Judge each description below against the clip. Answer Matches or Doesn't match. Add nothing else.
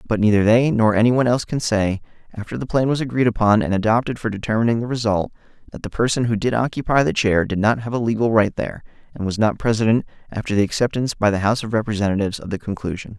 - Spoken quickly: Matches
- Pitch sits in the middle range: Doesn't match